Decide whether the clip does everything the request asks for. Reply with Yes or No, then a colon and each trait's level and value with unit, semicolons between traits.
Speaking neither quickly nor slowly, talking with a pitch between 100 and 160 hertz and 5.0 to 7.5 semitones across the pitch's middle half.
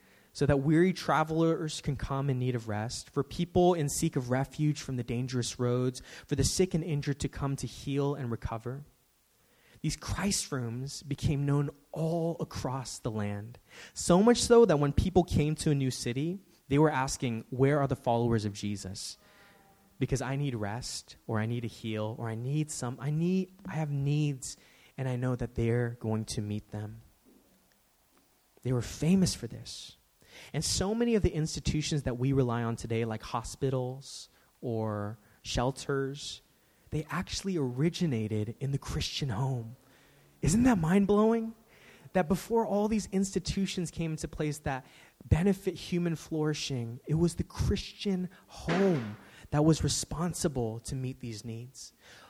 Yes: average, 165 wpm; medium, 140 Hz; average, 5.3 semitones